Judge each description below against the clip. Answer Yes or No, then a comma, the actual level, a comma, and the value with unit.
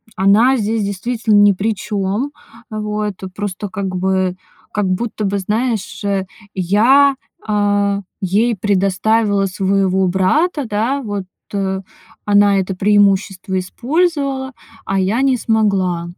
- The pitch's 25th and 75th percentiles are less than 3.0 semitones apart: Yes, narrow, 2.5 semitones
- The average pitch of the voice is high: Yes, high, 205 Hz